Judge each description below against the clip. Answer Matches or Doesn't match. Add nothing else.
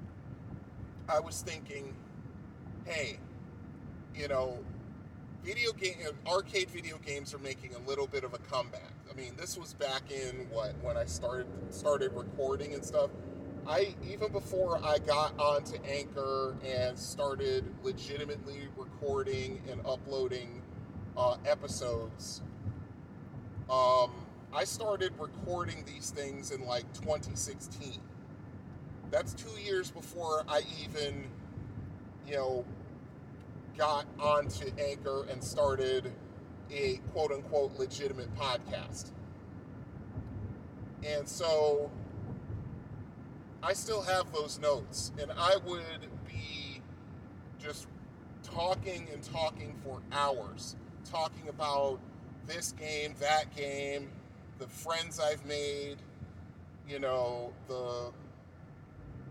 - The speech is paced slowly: Matches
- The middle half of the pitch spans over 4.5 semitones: Doesn't match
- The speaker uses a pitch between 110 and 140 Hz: Matches